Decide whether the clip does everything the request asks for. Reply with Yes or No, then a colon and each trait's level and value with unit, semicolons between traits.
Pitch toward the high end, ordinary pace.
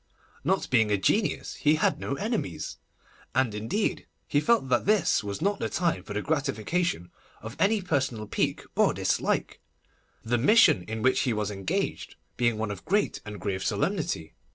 No: low, 130 Hz; average, 170 wpm